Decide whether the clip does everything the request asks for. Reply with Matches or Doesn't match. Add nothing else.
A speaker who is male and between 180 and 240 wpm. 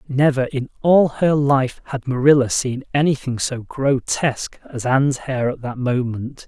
Doesn't match